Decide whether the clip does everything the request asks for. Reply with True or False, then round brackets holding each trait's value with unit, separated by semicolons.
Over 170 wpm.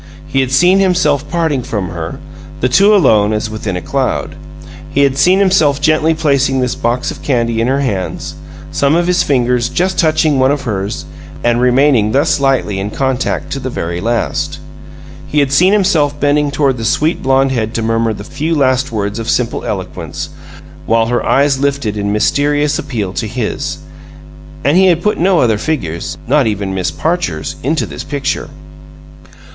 True (180 wpm)